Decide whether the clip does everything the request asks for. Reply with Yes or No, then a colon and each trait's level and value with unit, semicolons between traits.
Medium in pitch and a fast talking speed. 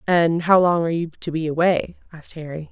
Yes: medium, 165 Hz; fast, 220 wpm